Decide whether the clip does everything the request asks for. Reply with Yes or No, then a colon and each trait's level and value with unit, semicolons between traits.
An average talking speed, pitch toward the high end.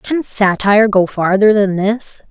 Yes: average, 155 wpm; high, 205 Hz